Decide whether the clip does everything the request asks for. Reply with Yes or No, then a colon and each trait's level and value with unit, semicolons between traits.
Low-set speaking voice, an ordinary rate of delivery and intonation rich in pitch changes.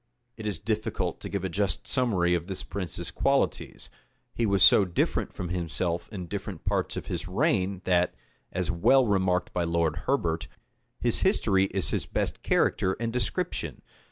No: very low, 95 Hz; average, 170 wpm; average, 3.1 semitones